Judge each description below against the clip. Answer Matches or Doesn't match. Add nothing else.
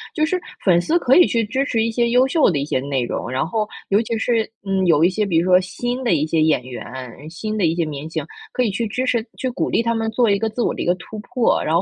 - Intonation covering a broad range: Matches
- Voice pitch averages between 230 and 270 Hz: Doesn't match